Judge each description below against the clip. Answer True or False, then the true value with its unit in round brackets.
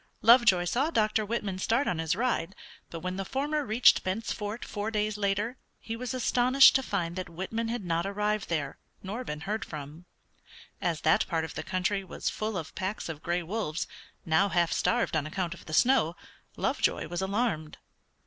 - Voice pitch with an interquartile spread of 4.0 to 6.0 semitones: True (5.0 semitones)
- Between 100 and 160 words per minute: False (185 wpm)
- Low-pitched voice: False (195 Hz)